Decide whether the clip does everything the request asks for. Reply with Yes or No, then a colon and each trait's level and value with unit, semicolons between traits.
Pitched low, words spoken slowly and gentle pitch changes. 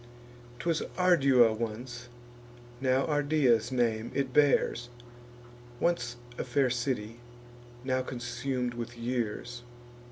Yes: low, 125 Hz; slow, 95 wpm; narrow, 2.2 semitones